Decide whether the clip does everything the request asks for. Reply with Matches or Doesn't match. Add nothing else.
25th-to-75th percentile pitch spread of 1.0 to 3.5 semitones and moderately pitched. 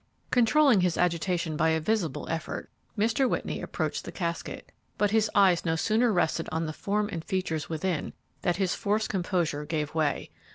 Doesn't match